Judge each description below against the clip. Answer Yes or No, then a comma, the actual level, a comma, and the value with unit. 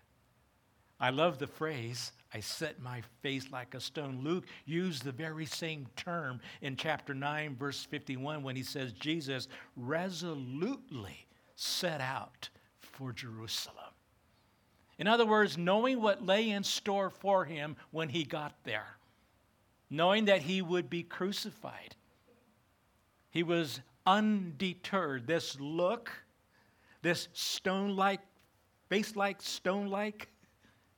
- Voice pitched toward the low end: No, medium, 155 Hz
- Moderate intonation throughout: No, wide, 6.7 semitones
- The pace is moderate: No, slow, 120 wpm